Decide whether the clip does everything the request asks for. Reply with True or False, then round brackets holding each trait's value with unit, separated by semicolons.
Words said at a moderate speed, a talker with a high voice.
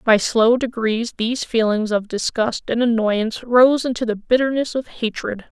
True (160 wpm; 230 Hz)